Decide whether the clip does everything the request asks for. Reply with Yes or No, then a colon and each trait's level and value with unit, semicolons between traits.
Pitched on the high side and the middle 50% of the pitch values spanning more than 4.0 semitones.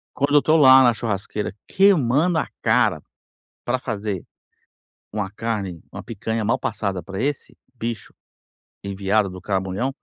No: low, 110 Hz; average, 4.8 semitones